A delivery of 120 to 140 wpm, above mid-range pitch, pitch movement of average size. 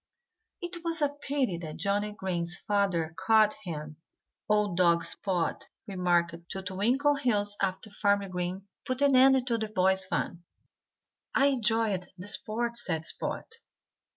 Yes: slow, 135 wpm; high, 200 Hz; average, 4.7 semitones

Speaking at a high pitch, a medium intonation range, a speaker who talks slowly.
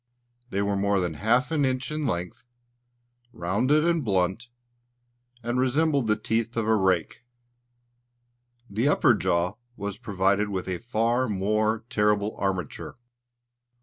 No: low, 110 Hz; average, 4.1 semitones; slow, 130 wpm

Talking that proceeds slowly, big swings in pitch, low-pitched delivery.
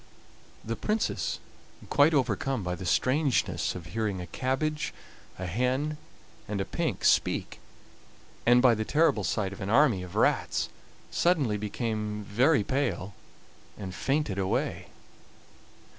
Yes: slow, 130 wpm; wide, 5.9 semitones; low, 115 Hz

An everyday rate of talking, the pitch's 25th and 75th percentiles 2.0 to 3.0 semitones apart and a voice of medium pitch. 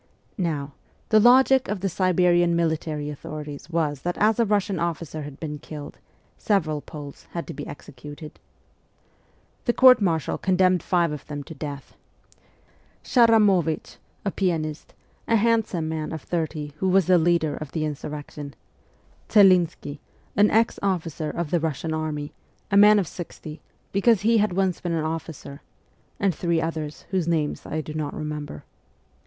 No: average, 160 wpm; average, 4.0 semitones; medium, 165 Hz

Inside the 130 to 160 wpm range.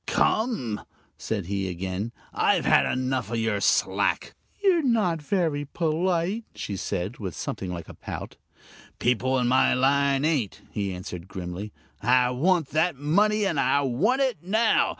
Yes: average, 155 wpm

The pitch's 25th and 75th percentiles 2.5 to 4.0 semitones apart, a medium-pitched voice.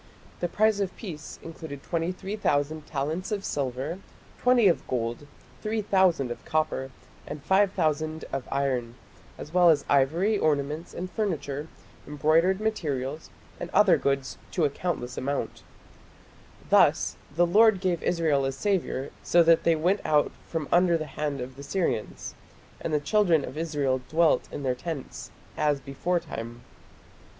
No: average, 4.4 semitones; medium, 155 Hz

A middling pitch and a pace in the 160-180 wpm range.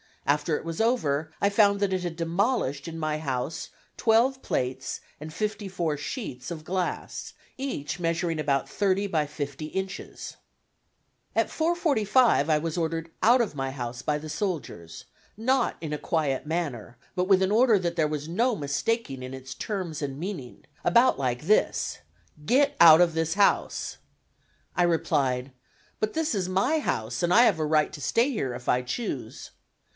Yes: medium, 165 Hz; average, 170 wpm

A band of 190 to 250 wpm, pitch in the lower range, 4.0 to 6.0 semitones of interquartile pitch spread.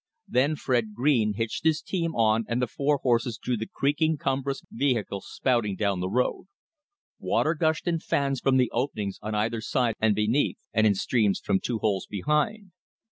No: average, 180 wpm; low, 120 Hz; average, 4.8 semitones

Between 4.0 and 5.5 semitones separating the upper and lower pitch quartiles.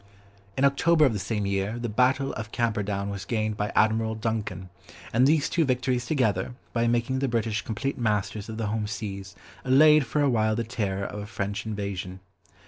No: average, 3.5 semitones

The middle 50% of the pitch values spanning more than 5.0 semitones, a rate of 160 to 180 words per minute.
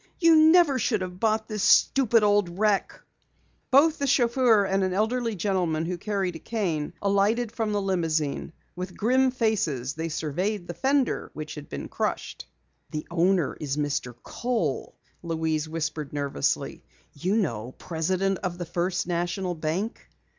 No: wide, 5.4 semitones; average, 150 wpm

